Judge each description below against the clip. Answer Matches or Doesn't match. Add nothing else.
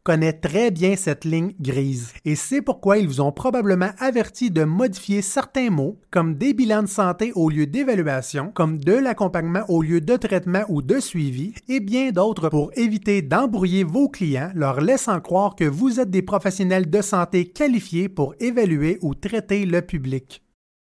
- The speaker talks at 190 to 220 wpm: Doesn't match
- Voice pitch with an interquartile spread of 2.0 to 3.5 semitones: Doesn't match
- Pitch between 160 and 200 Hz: Matches